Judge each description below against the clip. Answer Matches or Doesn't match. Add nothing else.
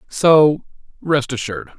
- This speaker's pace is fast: Doesn't match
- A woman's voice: Doesn't match